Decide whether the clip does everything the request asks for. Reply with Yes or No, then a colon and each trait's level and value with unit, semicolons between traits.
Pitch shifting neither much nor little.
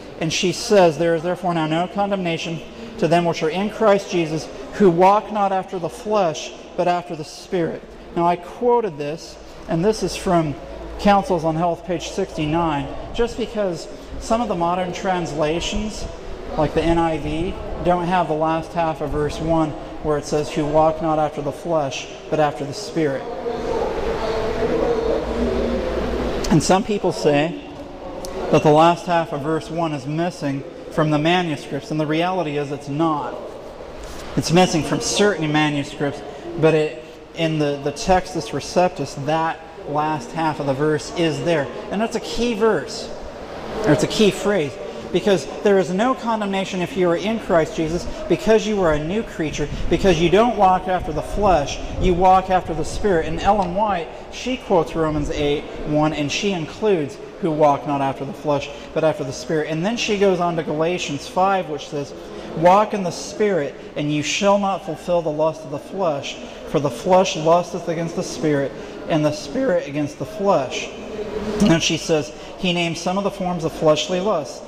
Yes: average, 3.9 semitones